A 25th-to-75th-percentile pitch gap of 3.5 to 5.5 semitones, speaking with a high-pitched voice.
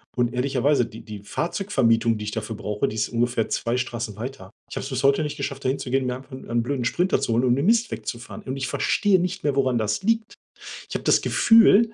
No: average, 3.8 semitones; low, 130 Hz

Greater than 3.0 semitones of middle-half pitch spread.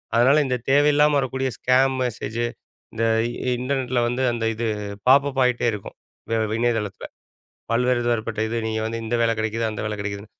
No: average, 2.7 semitones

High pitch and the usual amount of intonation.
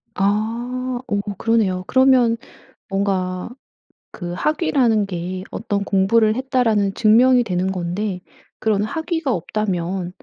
Yes: high, 205 Hz; average, 3.8 semitones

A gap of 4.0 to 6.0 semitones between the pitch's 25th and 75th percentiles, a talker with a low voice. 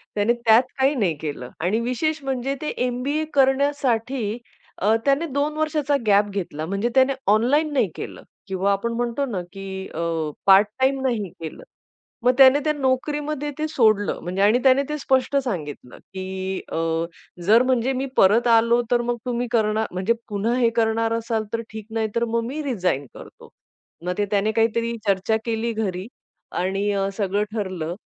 No: average, 4.7 semitones; high, 230 Hz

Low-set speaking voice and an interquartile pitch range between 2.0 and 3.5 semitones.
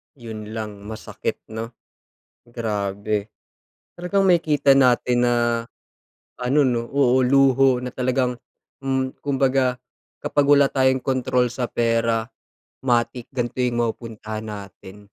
Yes: low, 125 Hz; average, 2.9 semitones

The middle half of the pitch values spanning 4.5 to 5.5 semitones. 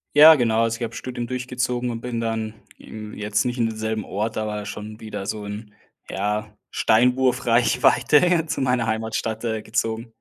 No: narrow, 2.4 semitones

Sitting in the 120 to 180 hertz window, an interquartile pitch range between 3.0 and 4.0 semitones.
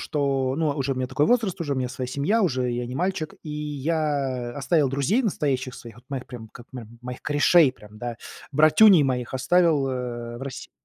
Yes: low, 135 Hz; average, 3.5 semitones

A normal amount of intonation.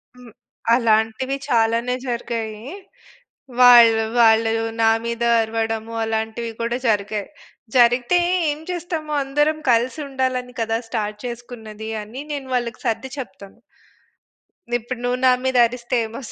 No: narrow, 2.2 semitones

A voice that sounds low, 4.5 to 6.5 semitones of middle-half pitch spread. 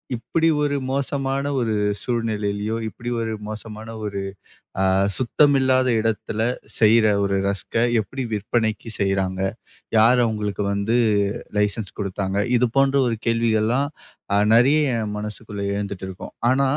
No: low, 110 Hz; average, 3.4 semitones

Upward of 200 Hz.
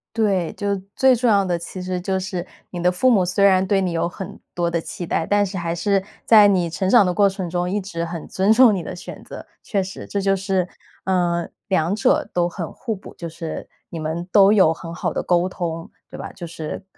No: medium, 185 Hz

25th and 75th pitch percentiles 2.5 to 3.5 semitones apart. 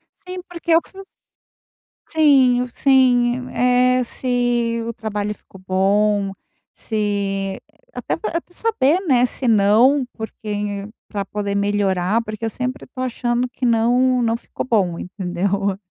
No: average, 3.9 semitones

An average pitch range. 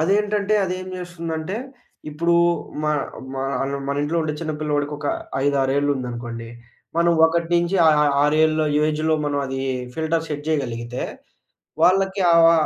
Yes: average, 3.0 semitones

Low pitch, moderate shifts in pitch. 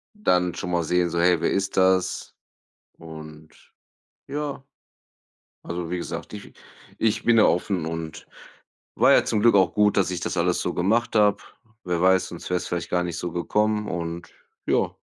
Yes: very low, 90 Hz; average, 3.2 semitones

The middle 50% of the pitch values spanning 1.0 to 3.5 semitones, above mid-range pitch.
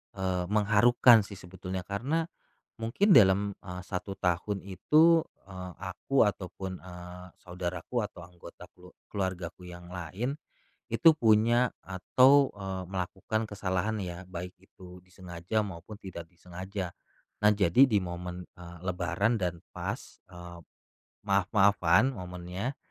No: average, 2.9 semitones; very low, 95 Hz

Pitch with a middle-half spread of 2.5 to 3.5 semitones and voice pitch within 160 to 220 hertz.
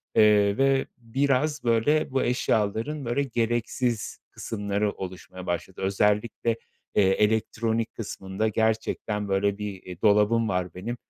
No: average, 2.8 semitones; low, 110 Hz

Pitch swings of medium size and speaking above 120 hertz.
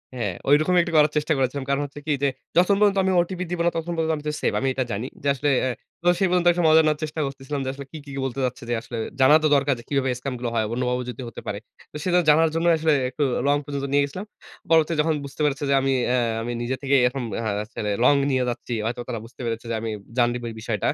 Yes: average, 4.1 semitones; medium, 140 Hz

